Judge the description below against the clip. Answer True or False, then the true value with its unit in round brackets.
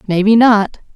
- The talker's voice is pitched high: True (210 Hz)